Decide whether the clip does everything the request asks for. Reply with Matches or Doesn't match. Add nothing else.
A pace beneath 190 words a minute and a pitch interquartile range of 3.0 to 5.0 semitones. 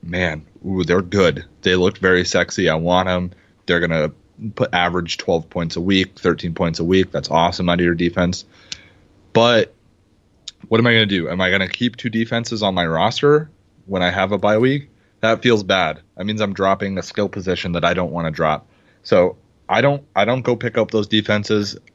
Doesn't match